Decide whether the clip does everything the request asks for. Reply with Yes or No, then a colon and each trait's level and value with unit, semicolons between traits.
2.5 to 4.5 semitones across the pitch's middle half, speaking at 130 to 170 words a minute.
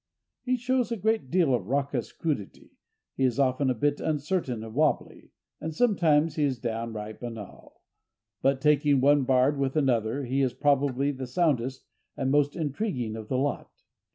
Yes: average, 3.2 semitones; average, 160 wpm